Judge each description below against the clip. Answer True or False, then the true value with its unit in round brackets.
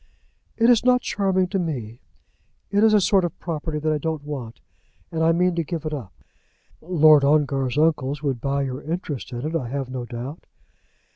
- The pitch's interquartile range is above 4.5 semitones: False (4.0 semitones)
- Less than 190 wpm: False (195 wpm)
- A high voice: False (155 Hz)